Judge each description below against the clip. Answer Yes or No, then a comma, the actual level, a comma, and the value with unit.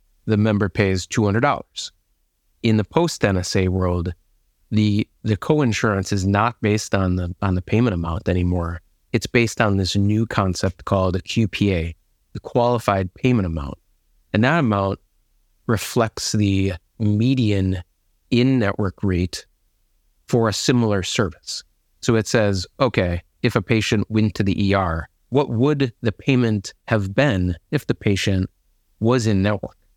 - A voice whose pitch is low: Yes, low, 105 Hz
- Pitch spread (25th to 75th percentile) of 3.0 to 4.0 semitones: Yes, average, 3.7 semitones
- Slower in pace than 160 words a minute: Yes, average, 140 wpm